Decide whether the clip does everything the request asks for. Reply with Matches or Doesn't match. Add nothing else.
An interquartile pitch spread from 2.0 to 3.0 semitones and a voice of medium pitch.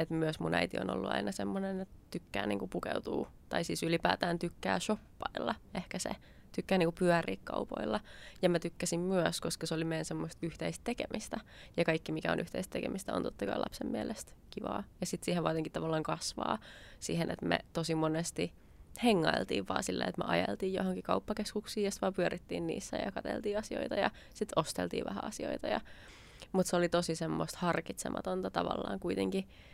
Matches